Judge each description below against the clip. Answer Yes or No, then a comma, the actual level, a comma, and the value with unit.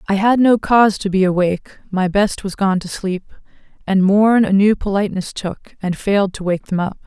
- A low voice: No, high, 195 Hz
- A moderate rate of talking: No, fast, 210 wpm